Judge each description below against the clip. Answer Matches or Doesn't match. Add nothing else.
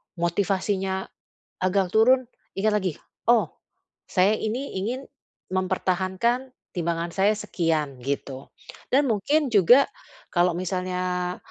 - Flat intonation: Doesn't match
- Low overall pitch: Doesn't match